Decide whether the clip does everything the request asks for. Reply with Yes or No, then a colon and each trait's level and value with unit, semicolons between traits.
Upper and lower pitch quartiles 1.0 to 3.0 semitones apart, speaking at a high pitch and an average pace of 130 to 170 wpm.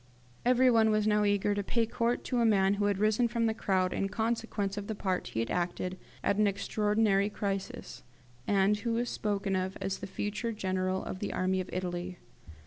No: narrow, 2.6 semitones; high, 205 Hz; average, 200 wpm